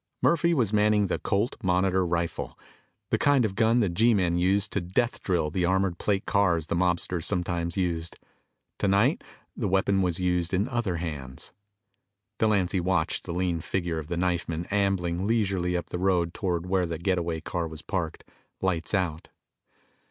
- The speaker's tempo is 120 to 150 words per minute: No, average, 165 wpm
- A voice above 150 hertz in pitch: No, very low, 90 Hz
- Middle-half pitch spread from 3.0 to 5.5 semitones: No, narrow, 2.6 semitones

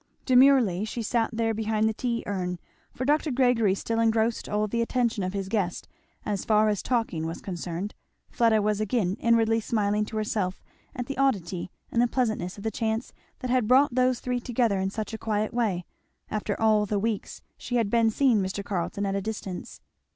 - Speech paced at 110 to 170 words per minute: No, average, 195 wpm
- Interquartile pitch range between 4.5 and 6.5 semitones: No, average, 2.8 semitones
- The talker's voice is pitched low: No, high, 220 Hz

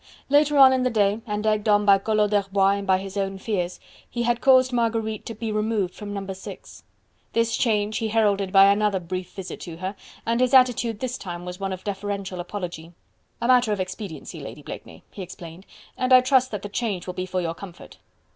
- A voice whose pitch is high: Yes, high, 205 Hz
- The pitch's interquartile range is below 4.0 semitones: Yes, average, 3.3 semitones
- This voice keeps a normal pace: No, fast, 210 wpm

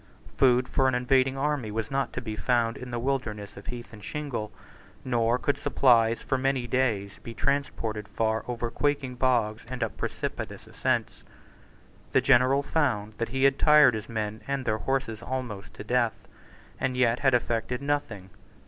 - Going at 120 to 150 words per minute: No, average, 170 wpm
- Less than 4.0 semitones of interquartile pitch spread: Yes, average, 2.9 semitones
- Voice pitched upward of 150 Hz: No, low, 125 Hz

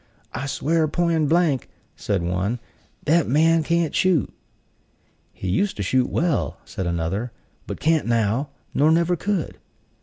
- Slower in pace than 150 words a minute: Yes, average, 140 wpm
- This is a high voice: No, medium, 150 Hz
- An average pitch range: No, wide, 6.8 semitones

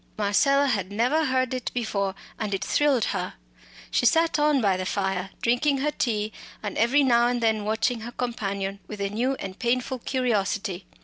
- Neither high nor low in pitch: No, high, 230 Hz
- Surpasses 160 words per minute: Yes, average, 180 wpm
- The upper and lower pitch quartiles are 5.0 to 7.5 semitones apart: No, average, 4.4 semitones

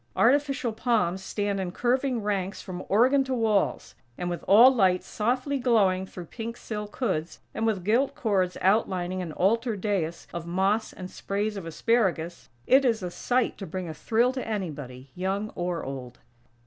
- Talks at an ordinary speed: Yes, average, 170 wpm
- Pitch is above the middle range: Yes, high, 200 Hz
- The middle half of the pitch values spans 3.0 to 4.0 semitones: No, average, 4.4 semitones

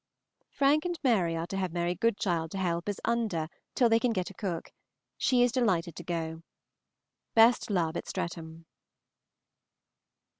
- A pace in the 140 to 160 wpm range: Yes, average, 155 wpm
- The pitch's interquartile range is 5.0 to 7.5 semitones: Yes, wide, 5.5 semitones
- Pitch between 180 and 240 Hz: Yes, medium, 185 Hz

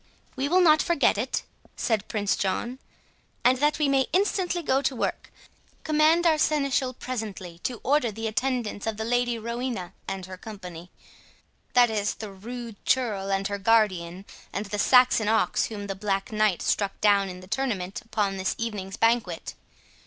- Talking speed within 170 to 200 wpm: No, average, 160 wpm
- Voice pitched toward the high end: Yes, high, 220 Hz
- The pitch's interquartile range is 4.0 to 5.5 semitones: Yes, average, 4.5 semitones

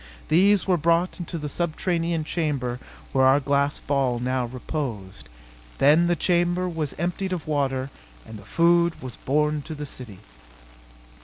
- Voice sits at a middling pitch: Yes, medium, 150 Hz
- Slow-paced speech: No, average, 150 wpm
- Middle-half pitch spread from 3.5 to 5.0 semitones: Yes, average, 4.5 semitones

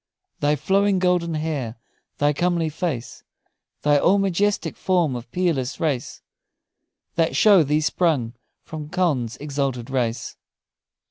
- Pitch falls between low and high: Yes, medium, 155 Hz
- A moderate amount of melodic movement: Yes, average, 4.9 semitones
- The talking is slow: Yes, slow, 120 wpm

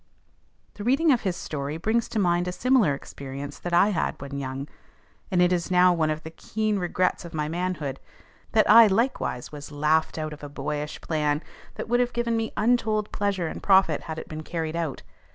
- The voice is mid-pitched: Yes, medium, 175 Hz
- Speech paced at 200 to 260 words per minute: Yes, fast, 205 wpm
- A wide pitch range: Yes, wide, 5.8 semitones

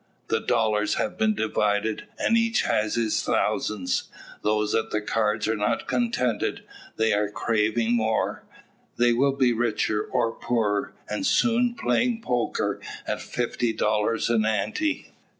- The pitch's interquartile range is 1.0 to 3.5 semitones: Yes, average, 2.9 semitones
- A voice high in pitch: No, low, 115 Hz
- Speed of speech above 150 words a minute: No, average, 140 wpm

